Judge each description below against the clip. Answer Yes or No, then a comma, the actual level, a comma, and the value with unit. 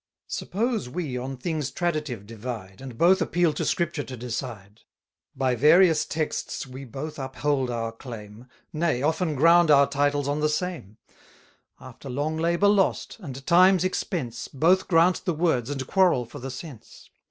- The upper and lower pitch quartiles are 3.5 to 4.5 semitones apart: No, wide, 5.4 semitones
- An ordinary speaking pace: Yes, average, 160 wpm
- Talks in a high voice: No, medium, 145 Hz